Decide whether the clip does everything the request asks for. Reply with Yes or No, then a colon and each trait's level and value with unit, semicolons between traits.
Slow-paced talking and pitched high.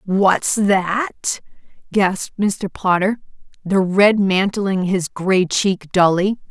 Yes: slow, 110 wpm; high, 195 Hz